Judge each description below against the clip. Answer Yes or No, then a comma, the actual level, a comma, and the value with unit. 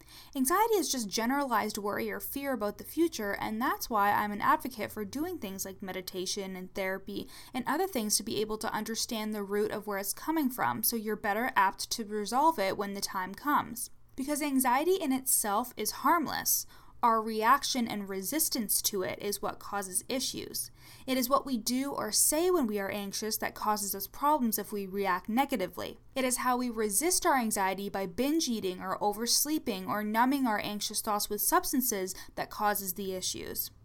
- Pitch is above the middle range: Yes, high, 215 Hz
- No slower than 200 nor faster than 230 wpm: No, average, 190 wpm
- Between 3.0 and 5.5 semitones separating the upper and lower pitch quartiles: Yes, average, 4.7 semitones